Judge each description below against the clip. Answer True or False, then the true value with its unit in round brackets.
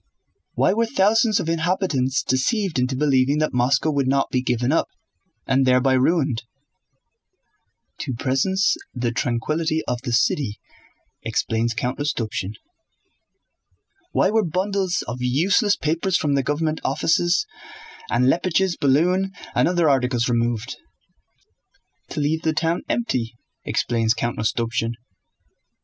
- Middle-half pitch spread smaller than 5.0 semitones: False (5.4 semitones)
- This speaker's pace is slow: True (120 wpm)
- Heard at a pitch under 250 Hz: True (140 Hz)